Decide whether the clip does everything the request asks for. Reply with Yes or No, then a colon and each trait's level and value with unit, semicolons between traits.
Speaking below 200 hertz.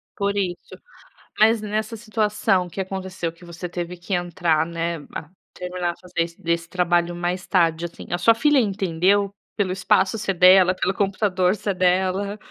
Yes: medium, 185 Hz